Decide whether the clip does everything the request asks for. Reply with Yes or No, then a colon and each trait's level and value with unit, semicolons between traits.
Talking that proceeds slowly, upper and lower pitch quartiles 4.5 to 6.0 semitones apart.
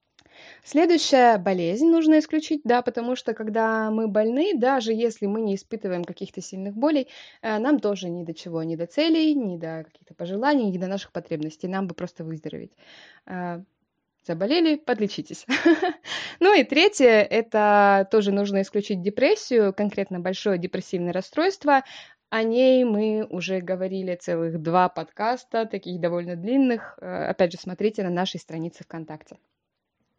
No: average, 140 wpm; wide, 5.6 semitones